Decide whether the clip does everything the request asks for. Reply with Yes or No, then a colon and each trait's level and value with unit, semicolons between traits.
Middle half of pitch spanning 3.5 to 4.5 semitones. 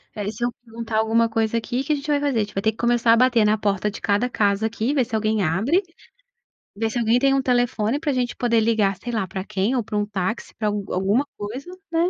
No: average, 2.7 semitones